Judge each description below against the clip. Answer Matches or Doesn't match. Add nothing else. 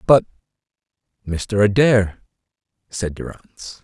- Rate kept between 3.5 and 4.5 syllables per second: Matches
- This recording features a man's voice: Matches